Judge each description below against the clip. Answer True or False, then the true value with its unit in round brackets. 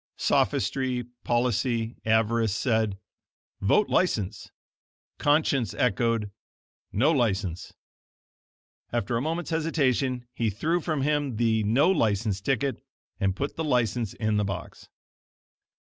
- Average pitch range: True (4.6 semitones)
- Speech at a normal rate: False (110 wpm)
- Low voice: True (120 Hz)